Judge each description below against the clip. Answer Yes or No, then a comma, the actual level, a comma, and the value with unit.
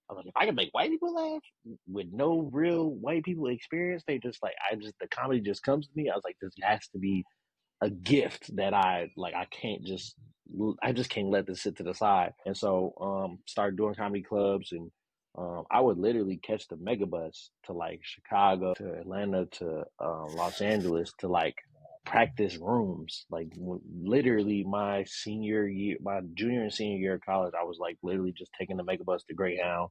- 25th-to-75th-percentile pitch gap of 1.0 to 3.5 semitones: No, average, 4.3 semitones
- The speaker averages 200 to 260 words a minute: Yes, fast, 205 wpm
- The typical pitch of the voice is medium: No, low, 100 Hz